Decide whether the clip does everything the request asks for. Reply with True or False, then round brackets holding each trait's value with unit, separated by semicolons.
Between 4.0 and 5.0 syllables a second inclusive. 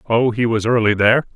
False (6.4 syllables/s)